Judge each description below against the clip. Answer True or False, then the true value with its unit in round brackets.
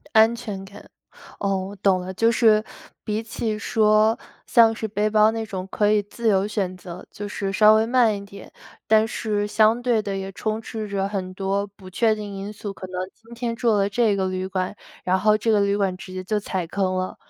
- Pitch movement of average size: False (2.1 semitones)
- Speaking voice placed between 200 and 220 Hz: True (205 Hz)